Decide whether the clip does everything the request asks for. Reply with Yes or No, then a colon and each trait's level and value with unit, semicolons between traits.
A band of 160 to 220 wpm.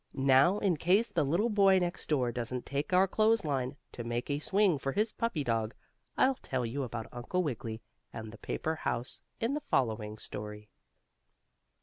Yes: average, 180 wpm